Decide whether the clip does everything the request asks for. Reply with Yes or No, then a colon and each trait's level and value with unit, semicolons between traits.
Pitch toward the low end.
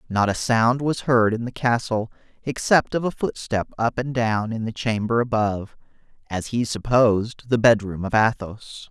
Yes: low, 115 Hz